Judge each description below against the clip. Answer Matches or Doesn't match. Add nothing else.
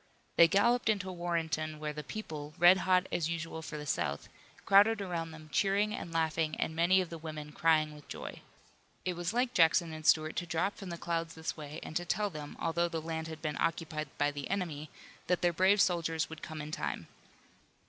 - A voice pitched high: Doesn't match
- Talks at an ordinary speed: Doesn't match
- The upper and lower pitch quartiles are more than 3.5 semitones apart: Doesn't match